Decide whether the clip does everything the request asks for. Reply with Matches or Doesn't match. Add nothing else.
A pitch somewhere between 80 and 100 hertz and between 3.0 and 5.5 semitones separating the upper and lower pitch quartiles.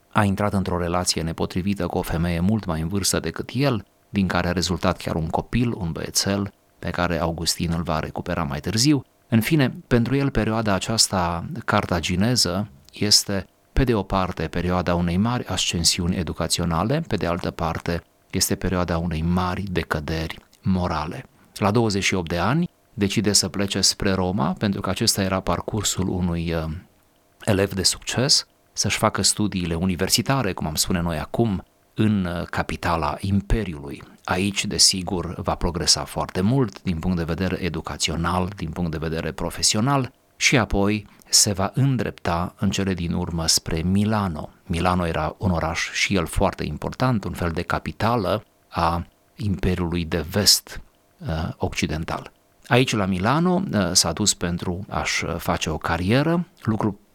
Matches